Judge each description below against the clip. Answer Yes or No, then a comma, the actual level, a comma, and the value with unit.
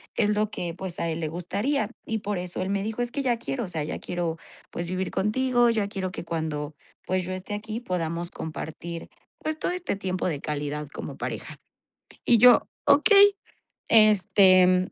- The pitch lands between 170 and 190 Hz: Yes, medium, 185 Hz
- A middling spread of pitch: Yes, average, 4.6 semitones